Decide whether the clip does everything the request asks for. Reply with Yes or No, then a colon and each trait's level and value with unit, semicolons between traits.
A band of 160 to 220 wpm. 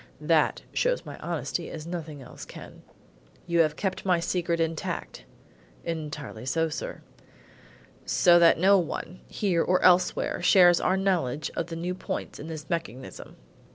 No: average, 150 wpm